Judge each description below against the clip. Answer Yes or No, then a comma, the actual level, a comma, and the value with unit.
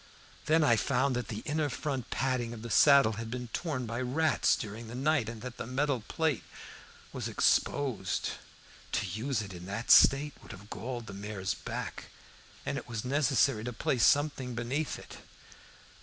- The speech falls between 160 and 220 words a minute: Yes, average, 175 wpm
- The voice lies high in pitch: No, low, 125 Hz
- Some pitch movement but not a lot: Yes, average, 4.0 semitones